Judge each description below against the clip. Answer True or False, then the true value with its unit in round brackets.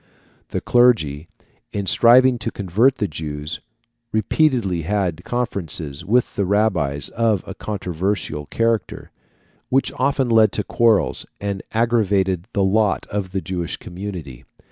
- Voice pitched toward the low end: True (100 Hz)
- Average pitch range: True (4.7 semitones)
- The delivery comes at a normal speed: False (125 wpm)